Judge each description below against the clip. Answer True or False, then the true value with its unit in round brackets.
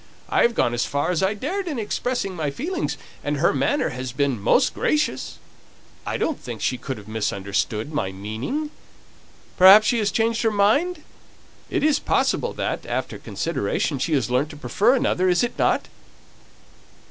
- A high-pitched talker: False (180 Hz)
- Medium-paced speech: True (170 wpm)